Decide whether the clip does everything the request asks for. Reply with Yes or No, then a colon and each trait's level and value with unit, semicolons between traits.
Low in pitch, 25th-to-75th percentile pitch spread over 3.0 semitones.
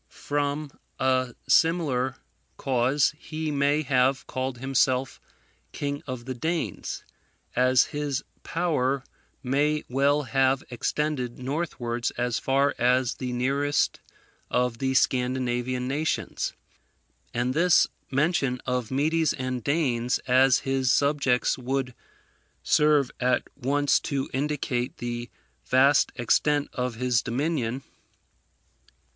No: low, 130 Hz; narrow, 2.5 semitones